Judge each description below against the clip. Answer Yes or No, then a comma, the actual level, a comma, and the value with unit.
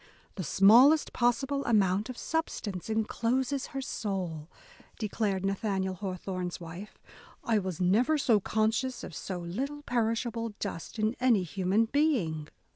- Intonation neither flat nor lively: Yes, average, 4.6 semitones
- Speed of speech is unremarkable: No, slow, 120 wpm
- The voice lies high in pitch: Yes, high, 215 Hz